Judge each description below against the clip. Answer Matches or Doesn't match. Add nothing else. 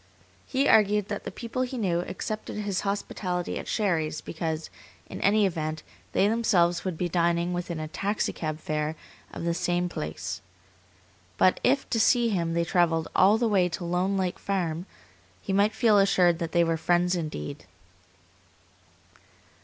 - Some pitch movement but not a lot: Matches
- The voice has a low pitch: Doesn't match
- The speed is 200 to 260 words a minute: Doesn't match